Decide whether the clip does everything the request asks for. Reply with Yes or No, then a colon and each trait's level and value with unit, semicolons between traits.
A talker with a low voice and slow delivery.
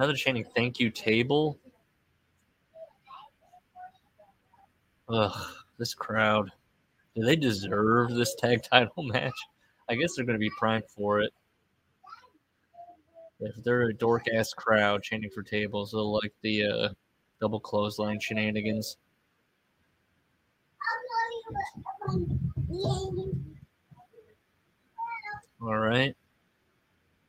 Yes: low, 115 Hz; slow, 90 wpm